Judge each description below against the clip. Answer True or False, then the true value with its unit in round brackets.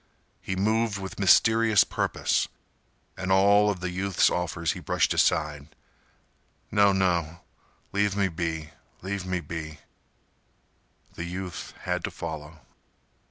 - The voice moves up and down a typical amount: True (3.4 semitones)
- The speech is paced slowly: True (110 wpm)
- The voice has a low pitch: True (95 Hz)